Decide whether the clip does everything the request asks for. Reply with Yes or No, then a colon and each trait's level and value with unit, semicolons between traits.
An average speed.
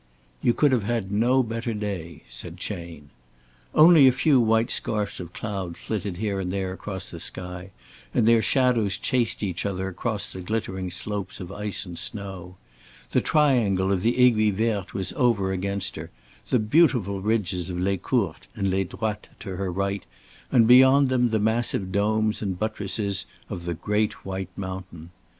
Yes: average, 170 wpm